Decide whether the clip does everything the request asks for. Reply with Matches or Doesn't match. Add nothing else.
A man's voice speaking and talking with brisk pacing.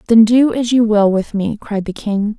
Doesn't match